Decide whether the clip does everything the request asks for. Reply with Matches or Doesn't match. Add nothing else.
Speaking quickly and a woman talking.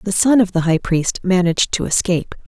Matches